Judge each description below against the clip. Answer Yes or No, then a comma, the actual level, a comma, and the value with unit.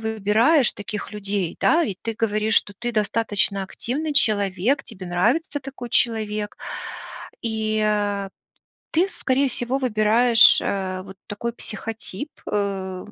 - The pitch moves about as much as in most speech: Yes, average, 3.0 semitones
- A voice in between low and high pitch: No, high, 215 Hz